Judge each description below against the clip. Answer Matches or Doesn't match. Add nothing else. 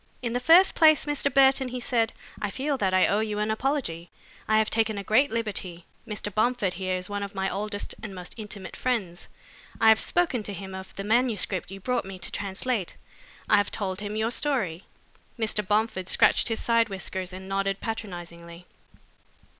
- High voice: Matches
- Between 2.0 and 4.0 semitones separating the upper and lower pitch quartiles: Matches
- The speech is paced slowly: Doesn't match